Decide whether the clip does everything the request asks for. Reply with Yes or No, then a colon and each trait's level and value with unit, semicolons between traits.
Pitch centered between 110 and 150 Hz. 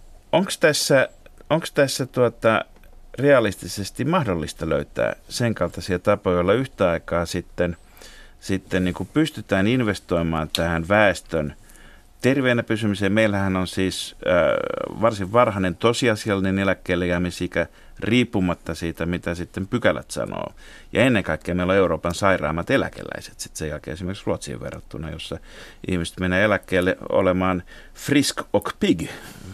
No: very low, 95 Hz